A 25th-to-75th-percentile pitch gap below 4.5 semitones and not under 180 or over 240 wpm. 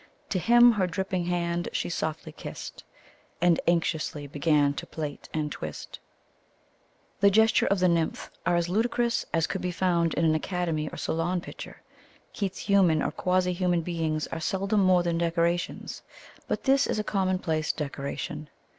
No: average, 2.8 semitones; average, 160 wpm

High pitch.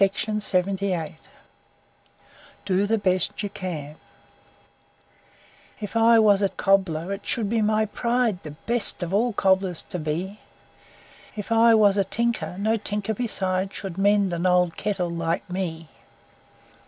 Yes: high, 195 Hz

